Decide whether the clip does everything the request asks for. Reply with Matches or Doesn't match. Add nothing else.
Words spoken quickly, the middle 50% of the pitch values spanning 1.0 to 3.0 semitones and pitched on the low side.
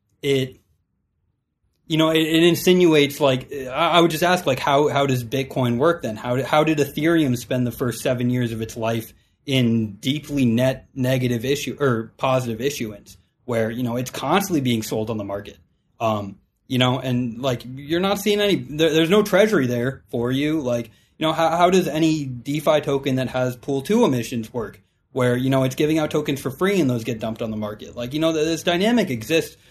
Doesn't match